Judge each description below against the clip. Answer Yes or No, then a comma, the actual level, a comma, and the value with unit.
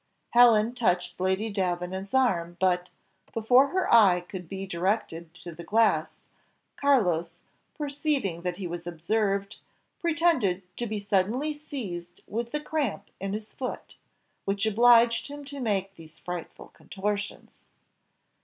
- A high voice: Yes, high, 200 Hz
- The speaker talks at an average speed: No, slow, 130 wpm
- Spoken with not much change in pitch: No, average, 5.2 semitones